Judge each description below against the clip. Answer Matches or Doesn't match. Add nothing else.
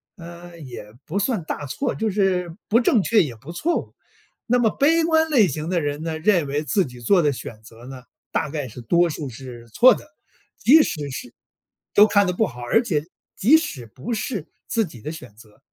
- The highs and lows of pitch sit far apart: Matches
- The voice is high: Doesn't match